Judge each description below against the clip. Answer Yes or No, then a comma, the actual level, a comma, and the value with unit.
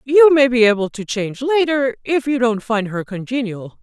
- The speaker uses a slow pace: No, fast, 205 wpm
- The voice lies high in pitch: Yes, high, 245 Hz